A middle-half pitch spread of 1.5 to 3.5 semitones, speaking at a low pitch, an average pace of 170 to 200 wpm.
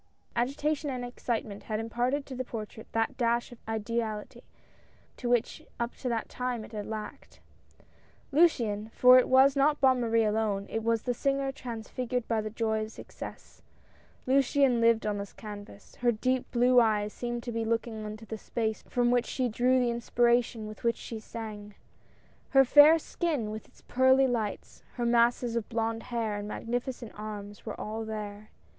No: narrow, 2.4 semitones; high, 235 Hz; average, 175 wpm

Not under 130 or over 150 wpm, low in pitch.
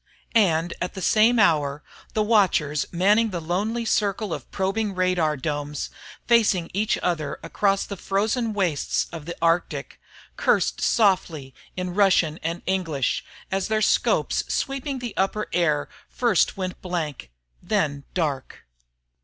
No: slow, 135 wpm; medium, 185 Hz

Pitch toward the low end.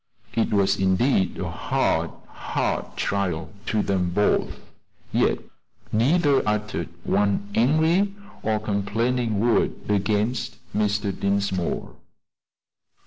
Yes: low, 105 Hz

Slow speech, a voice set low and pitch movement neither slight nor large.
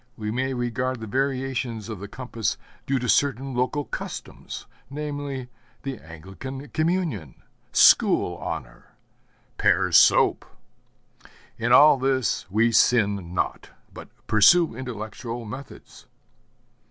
Yes: slow, 110 wpm; low, 125 Hz; average, 3.7 semitones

